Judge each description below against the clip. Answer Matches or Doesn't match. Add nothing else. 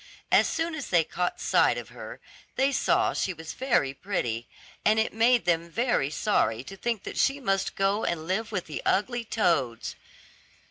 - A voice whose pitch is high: Matches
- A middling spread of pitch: Doesn't match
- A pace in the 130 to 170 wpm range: Doesn't match